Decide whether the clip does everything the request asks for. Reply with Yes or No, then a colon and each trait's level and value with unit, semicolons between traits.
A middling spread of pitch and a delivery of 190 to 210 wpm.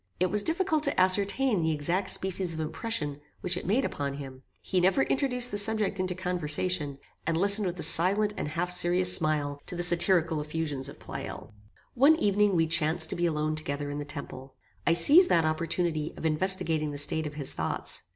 Yes: average, 4.0 semitones; average, 195 wpm